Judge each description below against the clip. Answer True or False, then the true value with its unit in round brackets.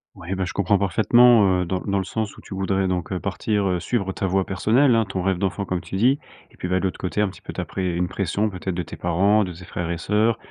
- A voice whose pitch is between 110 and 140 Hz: False (95 Hz)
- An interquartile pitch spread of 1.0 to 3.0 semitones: True (2.4 semitones)